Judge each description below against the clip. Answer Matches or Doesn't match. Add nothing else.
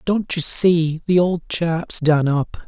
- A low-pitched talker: Doesn't match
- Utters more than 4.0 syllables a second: Doesn't match